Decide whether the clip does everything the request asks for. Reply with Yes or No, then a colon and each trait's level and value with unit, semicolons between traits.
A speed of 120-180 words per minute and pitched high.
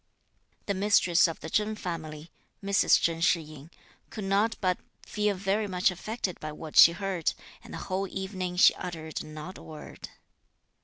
No: average, 165 wpm; medium, 180 Hz